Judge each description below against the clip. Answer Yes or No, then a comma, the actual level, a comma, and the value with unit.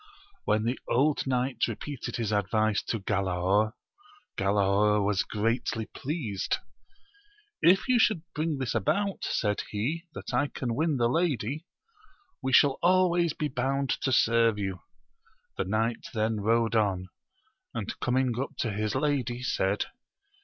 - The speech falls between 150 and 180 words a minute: No, slow, 135 wpm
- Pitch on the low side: Yes, low, 115 Hz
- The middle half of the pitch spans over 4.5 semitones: Yes, average, 4.9 semitones